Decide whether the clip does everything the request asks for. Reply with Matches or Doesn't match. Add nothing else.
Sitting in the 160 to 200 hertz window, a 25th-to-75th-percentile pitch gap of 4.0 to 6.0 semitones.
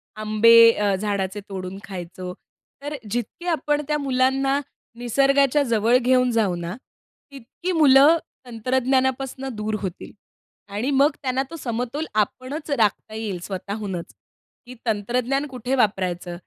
Doesn't match